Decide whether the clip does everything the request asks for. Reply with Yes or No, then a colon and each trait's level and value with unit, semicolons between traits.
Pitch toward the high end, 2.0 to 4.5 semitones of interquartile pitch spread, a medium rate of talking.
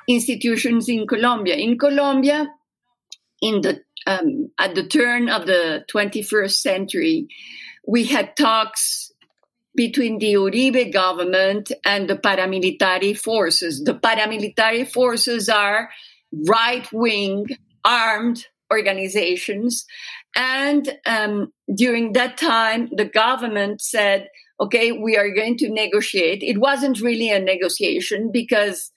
No: high, 230 Hz; average, 3.6 semitones; slow, 115 wpm